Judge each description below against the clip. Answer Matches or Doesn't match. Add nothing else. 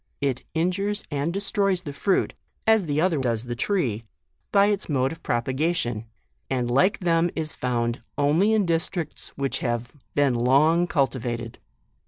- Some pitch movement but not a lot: Doesn't match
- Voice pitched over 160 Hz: Doesn't match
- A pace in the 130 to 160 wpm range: Matches